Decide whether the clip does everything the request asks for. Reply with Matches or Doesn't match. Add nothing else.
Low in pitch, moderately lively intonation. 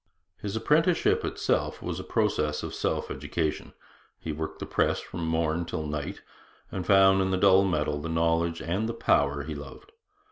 Matches